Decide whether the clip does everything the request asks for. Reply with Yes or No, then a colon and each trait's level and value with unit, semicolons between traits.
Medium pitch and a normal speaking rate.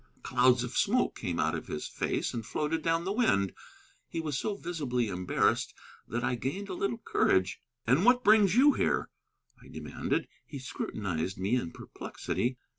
No: low, 130 Hz; average, 170 wpm